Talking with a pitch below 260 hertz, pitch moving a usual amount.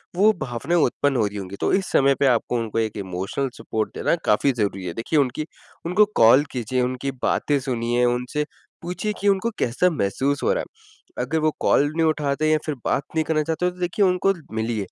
No: medium, 140 Hz; wide, 5.9 semitones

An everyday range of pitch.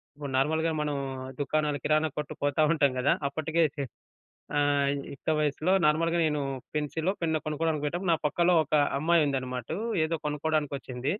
No: narrow, 2.0 semitones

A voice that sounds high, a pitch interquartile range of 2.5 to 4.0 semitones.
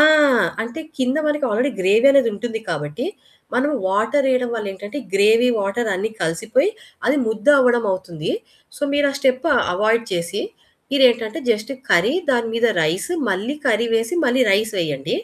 No: high, 225 Hz; average, 4.5 semitones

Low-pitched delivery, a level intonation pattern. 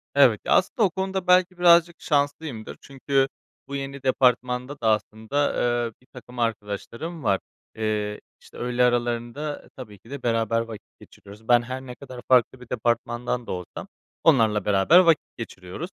No: low, 125 Hz; average, 4.0 semitones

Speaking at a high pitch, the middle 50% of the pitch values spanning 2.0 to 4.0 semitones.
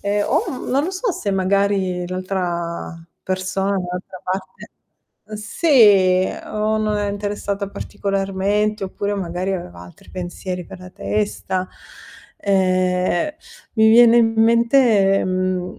Yes: high, 195 Hz; narrow, 2.4 semitones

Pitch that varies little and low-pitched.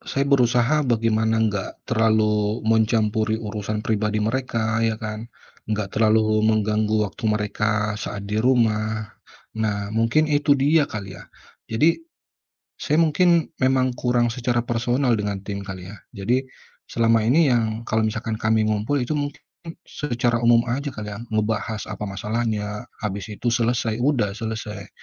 Yes: narrow, 2.2 semitones; low, 110 Hz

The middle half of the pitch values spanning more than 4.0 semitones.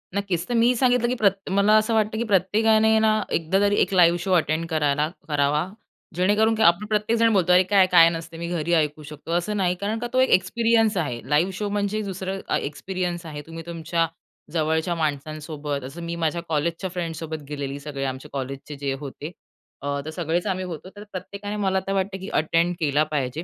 Yes: average, 4.6 semitones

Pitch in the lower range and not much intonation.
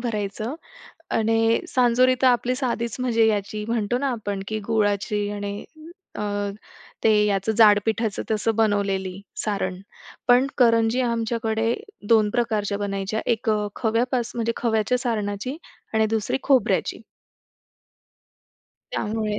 No: high, 220 Hz; narrow, 2.3 semitones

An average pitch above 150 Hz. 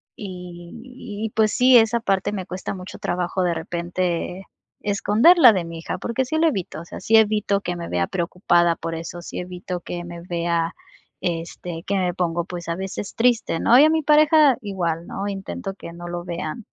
Yes: medium, 185 Hz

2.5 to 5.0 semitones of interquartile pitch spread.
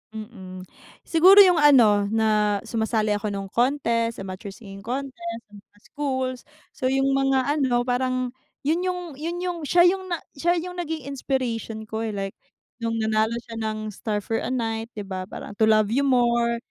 Yes: average, 4.2 semitones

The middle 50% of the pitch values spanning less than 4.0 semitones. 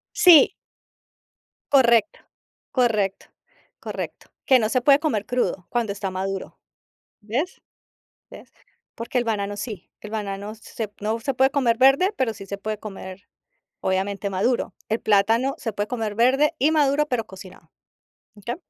No: average, 4.4 semitones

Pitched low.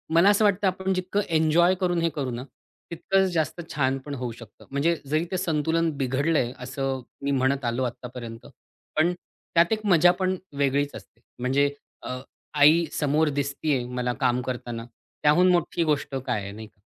No: medium, 145 Hz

